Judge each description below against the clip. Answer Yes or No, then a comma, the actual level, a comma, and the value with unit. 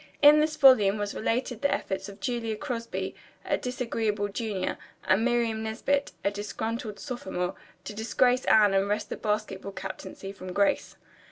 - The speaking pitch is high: Yes, high, 220 Hz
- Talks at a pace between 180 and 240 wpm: No, average, 155 wpm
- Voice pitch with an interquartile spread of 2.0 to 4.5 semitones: Yes, average, 3.5 semitones